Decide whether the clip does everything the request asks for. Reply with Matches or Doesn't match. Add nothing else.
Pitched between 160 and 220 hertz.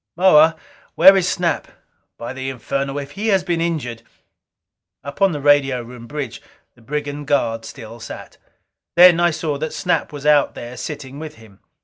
Doesn't match